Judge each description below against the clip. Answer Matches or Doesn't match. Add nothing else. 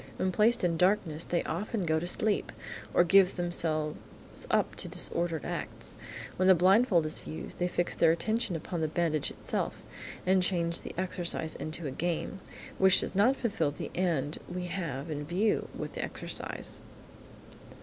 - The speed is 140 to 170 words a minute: Matches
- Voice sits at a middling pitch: Matches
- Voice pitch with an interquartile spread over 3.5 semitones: Doesn't match